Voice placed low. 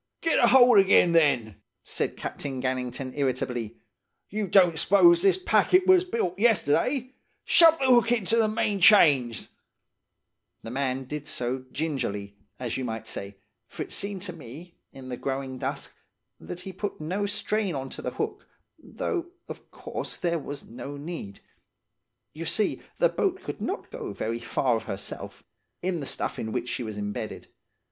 No: medium, 160 Hz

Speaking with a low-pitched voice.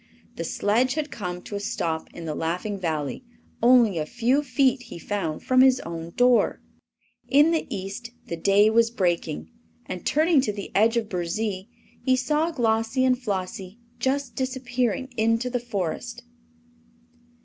No: high, 225 Hz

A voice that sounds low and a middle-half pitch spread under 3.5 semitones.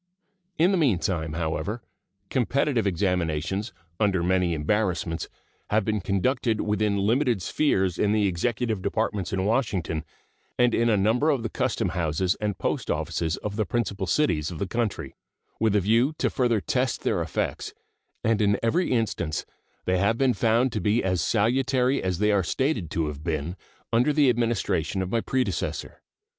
No: low, 105 Hz; average, 4.5 semitones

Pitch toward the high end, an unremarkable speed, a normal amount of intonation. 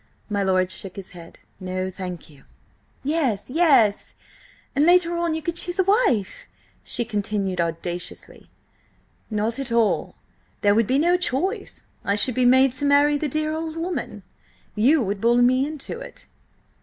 No: very high, 250 Hz; average, 160 wpm; wide, 7.7 semitones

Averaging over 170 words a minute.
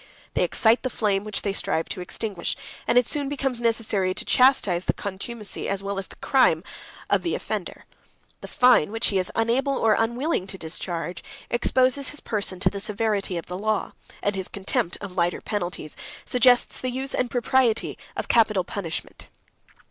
Yes: average, 180 wpm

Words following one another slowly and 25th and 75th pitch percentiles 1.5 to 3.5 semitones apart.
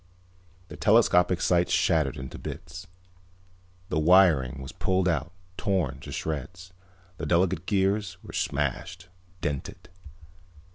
No: slow, 110 wpm; average, 3.9 semitones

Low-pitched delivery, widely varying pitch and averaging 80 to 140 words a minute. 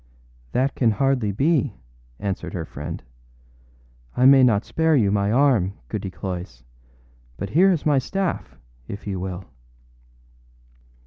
Yes: low, 110 Hz; wide, 6.5 semitones; slow, 135 wpm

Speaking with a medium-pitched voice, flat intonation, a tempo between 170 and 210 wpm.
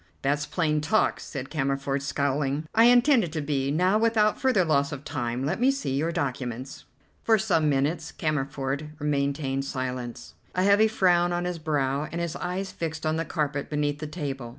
No: medium, 150 Hz; average, 4.2 semitones; average, 180 wpm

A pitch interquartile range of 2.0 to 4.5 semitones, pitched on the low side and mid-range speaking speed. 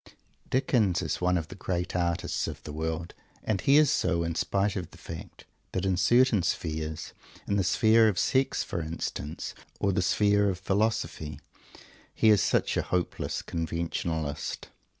Yes: average, 3.8 semitones; very low, 90 Hz; average, 165 wpm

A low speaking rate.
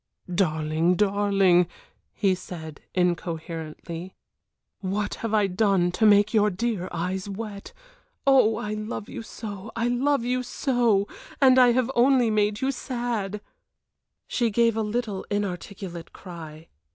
Yes: slow, 130 wpm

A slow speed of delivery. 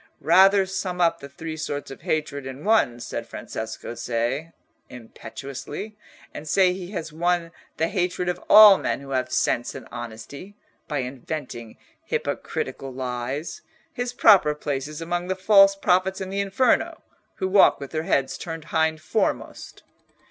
No: average, 155 wpm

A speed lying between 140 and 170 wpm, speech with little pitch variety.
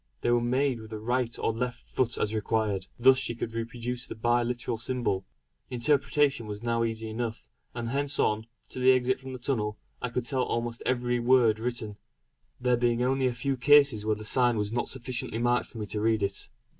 No: fast, 205 wpm; narrow, 2.3 semitones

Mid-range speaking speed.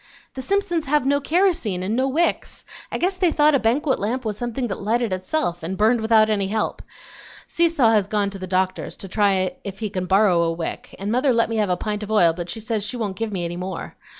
No: fast, 240 wpm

